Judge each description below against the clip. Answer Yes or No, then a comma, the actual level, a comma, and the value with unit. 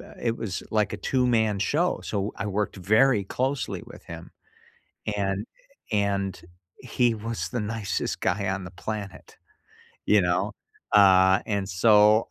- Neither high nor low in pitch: No, low, 105 Hz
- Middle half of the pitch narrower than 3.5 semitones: Yes, average, 2.7 semitones